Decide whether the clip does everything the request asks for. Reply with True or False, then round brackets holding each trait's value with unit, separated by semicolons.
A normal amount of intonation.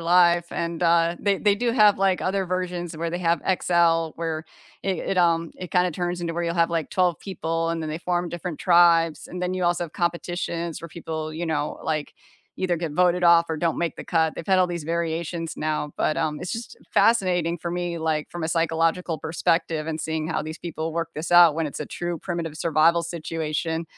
False (1.4 semitones)